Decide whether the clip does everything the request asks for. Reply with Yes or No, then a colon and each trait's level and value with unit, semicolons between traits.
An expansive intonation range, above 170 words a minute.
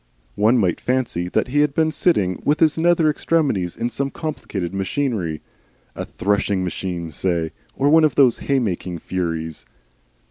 No: wide, 8.4 semitones; average, 155 wpm